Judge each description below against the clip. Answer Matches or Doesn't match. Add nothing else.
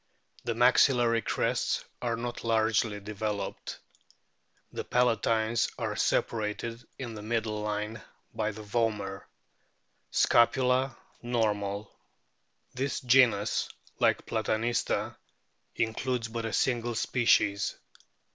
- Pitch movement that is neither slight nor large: Doesn't match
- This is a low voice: Matches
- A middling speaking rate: Doesn't match